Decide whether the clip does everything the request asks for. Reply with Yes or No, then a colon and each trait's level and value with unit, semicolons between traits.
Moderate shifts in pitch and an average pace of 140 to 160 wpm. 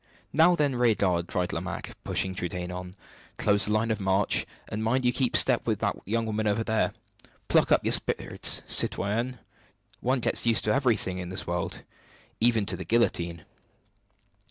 No: average, 4.3 semitones; average, 170 wpm